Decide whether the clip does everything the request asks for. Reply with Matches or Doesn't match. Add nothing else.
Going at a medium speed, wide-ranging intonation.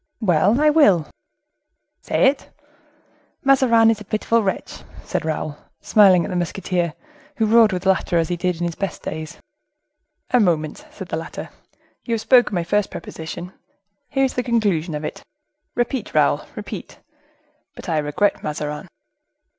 Matches